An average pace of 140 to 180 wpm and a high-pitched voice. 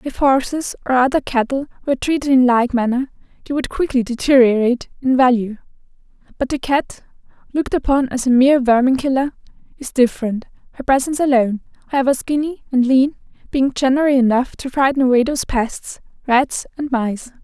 Yes: average, 160 wpm; very high, 260 Hz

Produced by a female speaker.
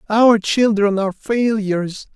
No: male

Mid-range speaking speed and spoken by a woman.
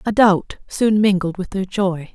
Yes: average, 195 wpm; female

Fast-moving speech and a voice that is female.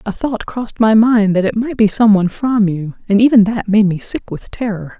Yes: fast, 250 wpm; female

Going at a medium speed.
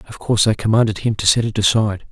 No: fast, 255 wpm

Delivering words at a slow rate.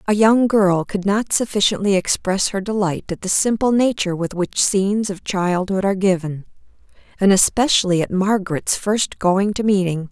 No: average, 165 wpm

